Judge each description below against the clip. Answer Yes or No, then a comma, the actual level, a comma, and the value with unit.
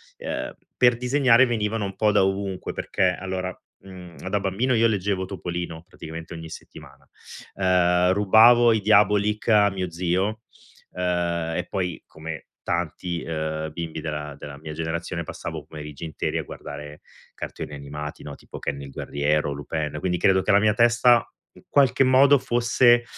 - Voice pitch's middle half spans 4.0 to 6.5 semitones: Yes, average, 4.7 semitones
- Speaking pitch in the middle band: No, very low, 90 Hz